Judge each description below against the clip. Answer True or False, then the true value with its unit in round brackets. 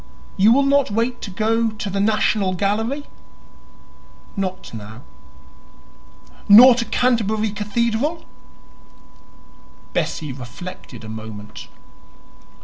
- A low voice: False (210 Hz)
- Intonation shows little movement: False (4.2 semitones)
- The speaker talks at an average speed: False (95 wpm)